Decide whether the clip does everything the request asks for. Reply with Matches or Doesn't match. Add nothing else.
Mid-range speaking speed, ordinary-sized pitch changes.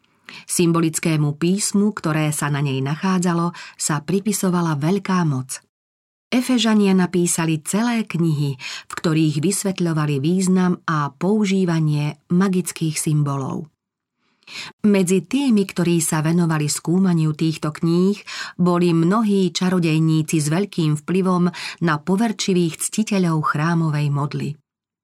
Doesn't match